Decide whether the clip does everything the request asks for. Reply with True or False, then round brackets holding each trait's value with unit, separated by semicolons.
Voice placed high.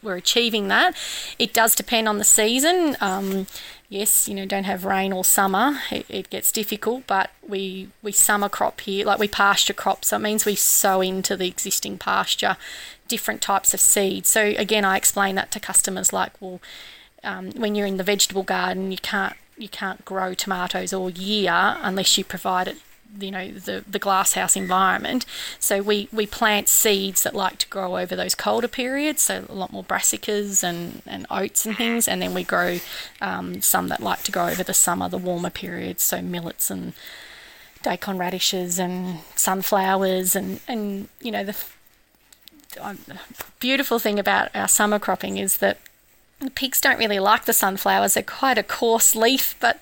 True (200 Hz)